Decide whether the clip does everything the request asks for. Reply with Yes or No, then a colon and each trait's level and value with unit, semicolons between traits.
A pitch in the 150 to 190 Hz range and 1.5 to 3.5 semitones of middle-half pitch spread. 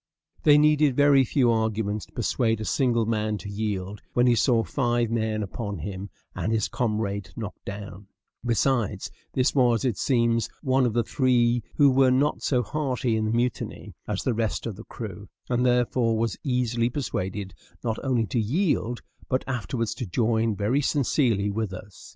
No: low, 115 Hz; average, 2.9 semitones